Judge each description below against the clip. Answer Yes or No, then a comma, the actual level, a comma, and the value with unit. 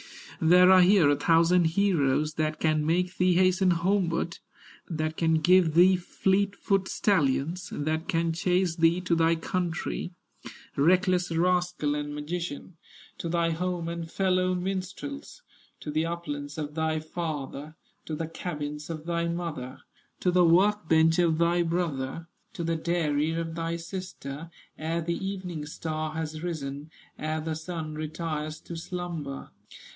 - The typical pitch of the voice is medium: Yes, medium, 165 Hz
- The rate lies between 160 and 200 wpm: No, average, 145 wpm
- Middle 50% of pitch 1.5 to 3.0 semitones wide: Yes, narrow, 2.4 semitones